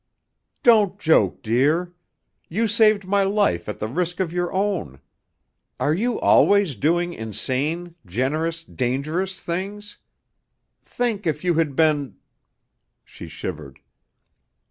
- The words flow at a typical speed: No, slow, 120 wpm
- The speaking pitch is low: No, medium, 170 Hz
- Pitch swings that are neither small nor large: No, wide, 6.1 semitones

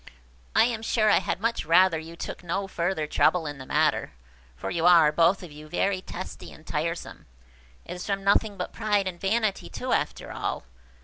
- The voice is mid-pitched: Yes, medium, 180 Hz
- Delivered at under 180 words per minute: No, average, 195 wpm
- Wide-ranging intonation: No, average, 3.3 semitones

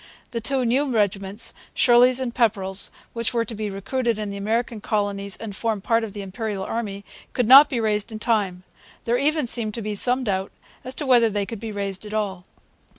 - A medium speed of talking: No, fast, 210 wpm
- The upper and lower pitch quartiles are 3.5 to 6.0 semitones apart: No, average, 3.0 semitones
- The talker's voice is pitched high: Yes, high, 220 Hz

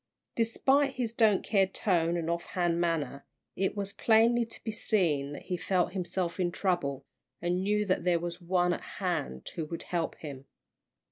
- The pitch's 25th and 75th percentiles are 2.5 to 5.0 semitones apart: Yes, average, 3.3 semitones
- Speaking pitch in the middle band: Yes, medium, 180 Hz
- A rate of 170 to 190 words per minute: Yes, average, 180 wpm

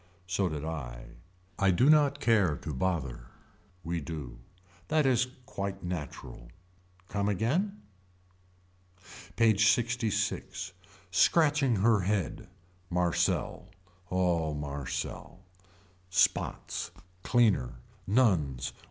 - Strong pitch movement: Yes, wide, 7.1 semitones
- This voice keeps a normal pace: No, slow, 90 wpm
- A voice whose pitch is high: No, very low, 95 Hz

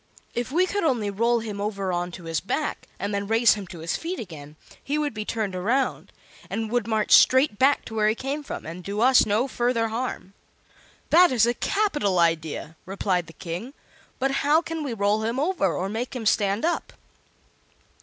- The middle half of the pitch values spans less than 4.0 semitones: No, average, 5.2 semitones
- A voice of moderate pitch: No, high, 220 Hz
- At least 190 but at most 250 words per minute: Yes, average, 200 wpm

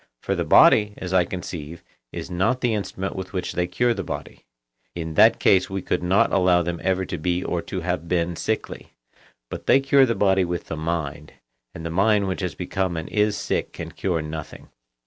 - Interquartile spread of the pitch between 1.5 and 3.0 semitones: Yes, narrow, 2.5 semitones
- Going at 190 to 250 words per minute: Yes, fast, 205 wpm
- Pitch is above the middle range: No, very low, 90 Hz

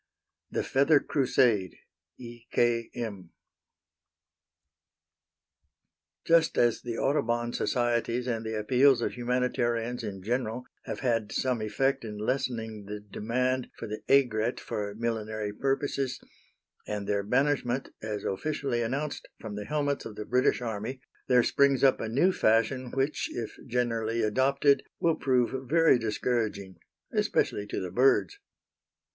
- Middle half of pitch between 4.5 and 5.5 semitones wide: No, average, 3.4 semitones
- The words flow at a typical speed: No, slow, 130 wpm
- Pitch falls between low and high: No, low, 120 Hz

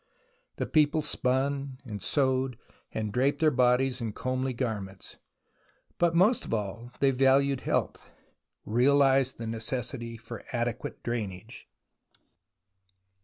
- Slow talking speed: Yes, slow, 115 wpm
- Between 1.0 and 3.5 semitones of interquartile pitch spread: Yes, average, 2.9 semitones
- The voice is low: Yes, low, 130 Hz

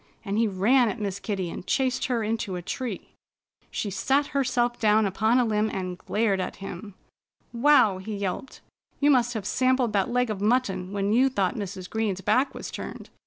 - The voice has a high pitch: Yes, high, 215 Hz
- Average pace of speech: Yes, average, 190 wpm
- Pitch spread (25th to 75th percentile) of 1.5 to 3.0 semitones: No, average, 4.1 semitones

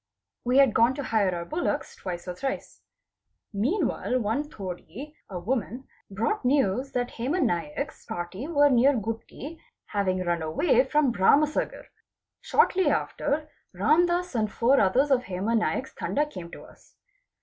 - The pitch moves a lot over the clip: Yes, wide, 7.0 semitones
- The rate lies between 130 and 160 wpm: Yes, average, 150 wpm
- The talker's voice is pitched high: Yes, high, 245 Hz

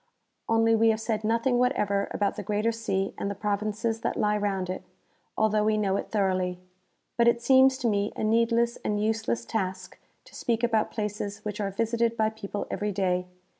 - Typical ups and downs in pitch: No, narrow, 2.1 semitones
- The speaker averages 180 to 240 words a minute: Yes, average, 195 wpm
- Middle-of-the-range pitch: No, high, 215 Hz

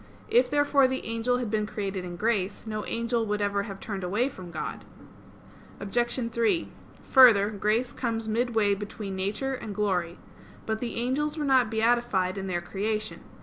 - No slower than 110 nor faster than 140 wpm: No, average, 165 wpm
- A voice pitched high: Yes, high, 220 Hz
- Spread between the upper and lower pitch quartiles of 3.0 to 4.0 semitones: Yes, average, 3.3 semitones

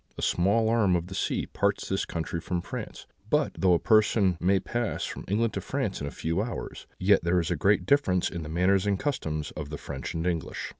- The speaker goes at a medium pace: No, fast, 230 wpm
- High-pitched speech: No, very low, 95 Hz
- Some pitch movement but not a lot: Yes, average, 3.5 semitones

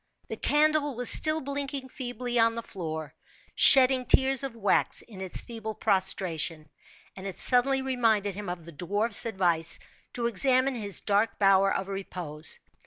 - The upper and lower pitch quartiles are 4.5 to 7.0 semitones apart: Yes, average, 5.3 semitones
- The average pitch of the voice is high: Yes, high, 220 Hz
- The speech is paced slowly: No, average, 155 wpm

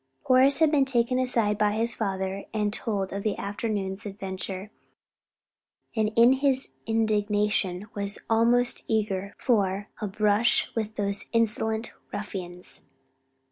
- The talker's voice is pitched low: No, high, 210 Hz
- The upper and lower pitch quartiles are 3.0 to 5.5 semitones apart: No, narrow, 2.6 semitones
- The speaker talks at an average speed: No, slow, 125 wpm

